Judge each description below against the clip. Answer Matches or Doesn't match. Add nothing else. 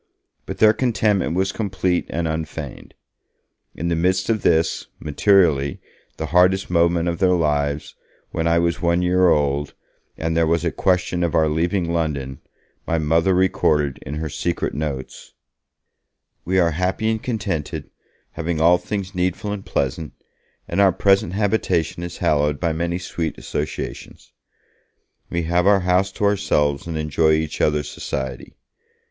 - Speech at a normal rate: Matches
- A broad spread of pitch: Doesn't match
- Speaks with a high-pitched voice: Doesn't match